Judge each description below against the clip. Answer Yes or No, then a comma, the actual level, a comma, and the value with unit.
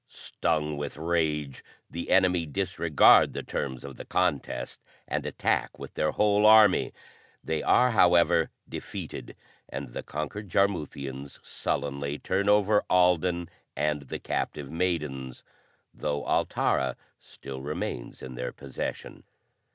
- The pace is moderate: No, slow, 120 wpm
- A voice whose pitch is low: Yes, very low, 75 Hz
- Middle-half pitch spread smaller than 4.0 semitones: No, average, 4.7 semitones